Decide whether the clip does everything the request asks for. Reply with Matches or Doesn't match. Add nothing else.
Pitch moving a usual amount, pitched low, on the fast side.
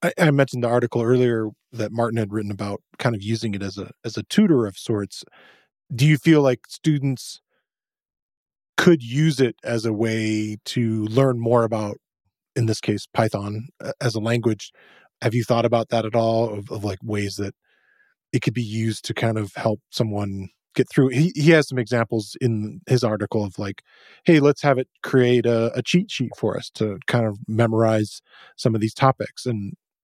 Doesn't match